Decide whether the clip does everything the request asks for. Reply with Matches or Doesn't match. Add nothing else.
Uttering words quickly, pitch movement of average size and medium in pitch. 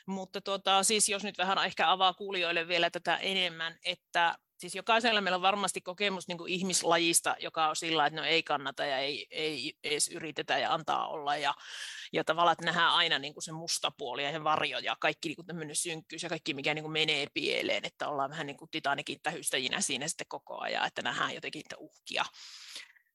Matches